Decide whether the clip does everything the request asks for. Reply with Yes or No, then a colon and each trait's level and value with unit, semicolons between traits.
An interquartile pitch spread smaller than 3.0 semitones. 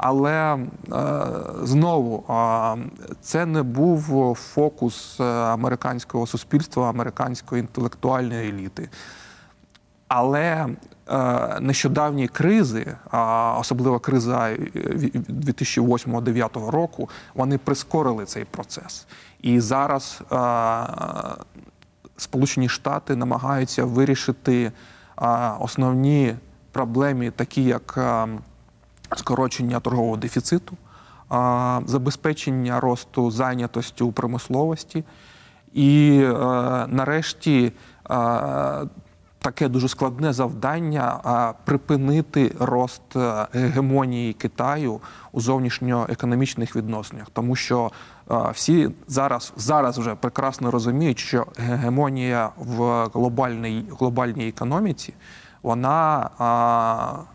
Yes: narrow, 2.5 semitones